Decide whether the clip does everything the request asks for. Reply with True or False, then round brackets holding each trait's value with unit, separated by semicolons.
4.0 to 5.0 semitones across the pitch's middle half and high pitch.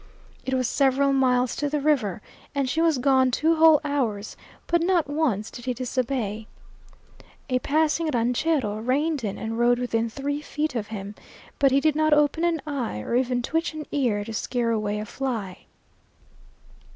True (4.5 semitones; 260 Hz)